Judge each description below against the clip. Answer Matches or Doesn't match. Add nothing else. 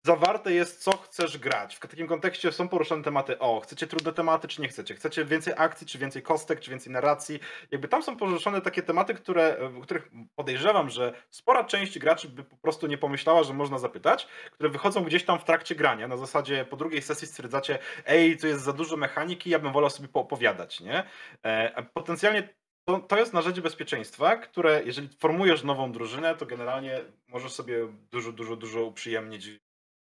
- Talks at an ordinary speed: Doesn't match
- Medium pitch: Matches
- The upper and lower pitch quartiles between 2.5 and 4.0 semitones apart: Doesn't match